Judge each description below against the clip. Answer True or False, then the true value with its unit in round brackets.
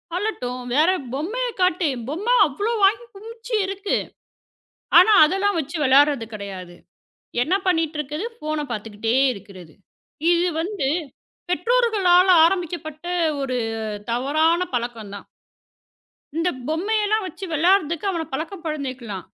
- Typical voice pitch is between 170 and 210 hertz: False (320 Hz)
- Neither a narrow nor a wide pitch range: False (6.6 semitones)